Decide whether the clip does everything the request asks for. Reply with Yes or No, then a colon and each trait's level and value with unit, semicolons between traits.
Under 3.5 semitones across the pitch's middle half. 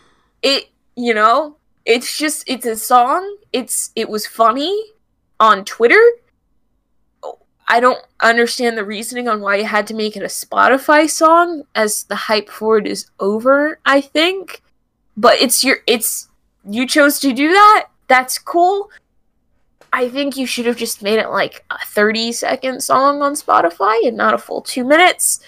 No: wide, 5.6 semitones